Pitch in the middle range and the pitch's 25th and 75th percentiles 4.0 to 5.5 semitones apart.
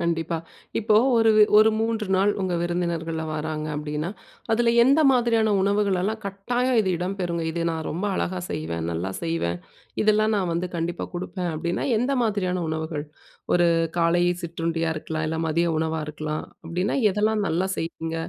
Yes: medium, 175 Hz; average, 4.3 semitones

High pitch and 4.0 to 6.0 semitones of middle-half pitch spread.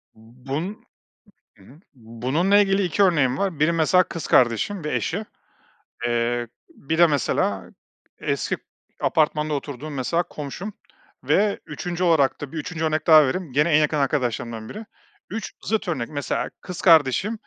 No: medium, 155 Hz; average, 5.3 semitones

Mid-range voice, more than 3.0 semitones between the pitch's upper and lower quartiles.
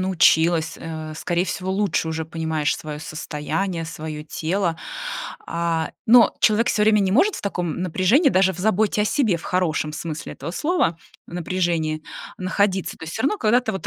Yes: medium, 175 Hz; average, 3.9 semitones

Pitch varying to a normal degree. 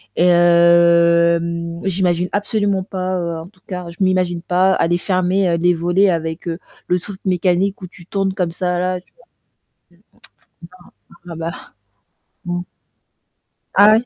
No: narrow, 1.7 semitones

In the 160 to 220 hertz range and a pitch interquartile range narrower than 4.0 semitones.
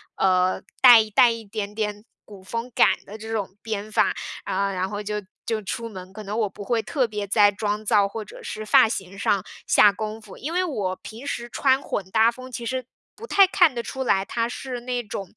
Yes: high, 215 Hz; average, 2.9 semitones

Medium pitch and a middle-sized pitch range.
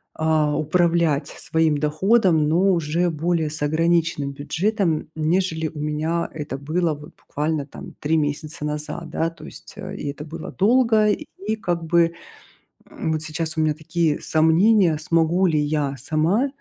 No: medium, 160 Hz; narrow, 2.3 semitones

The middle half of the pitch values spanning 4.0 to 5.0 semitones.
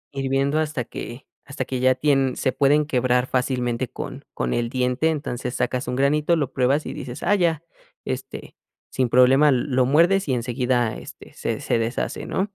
No: average, 3.0 semitones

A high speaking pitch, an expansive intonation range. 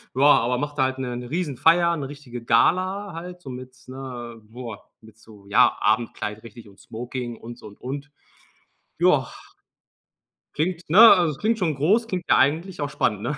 No: low, 130 Hz; wide, 5.8 semitones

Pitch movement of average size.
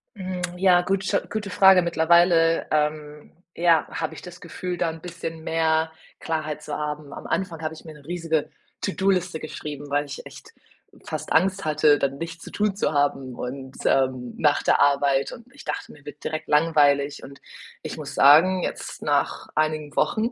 Yes: average, 3.3 semitones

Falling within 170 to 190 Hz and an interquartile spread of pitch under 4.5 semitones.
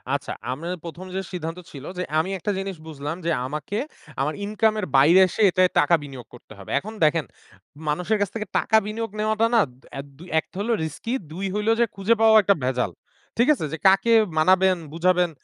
No: medium, 185 Hz; wide, 5.5 semitones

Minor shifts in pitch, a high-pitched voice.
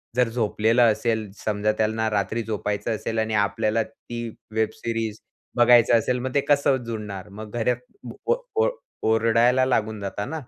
No: narrow, 2.2 semitones; low, 110 Hz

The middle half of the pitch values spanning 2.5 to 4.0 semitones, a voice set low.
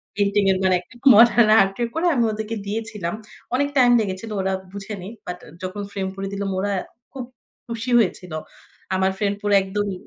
No: average, 2.9 semitones; high, 200 Hz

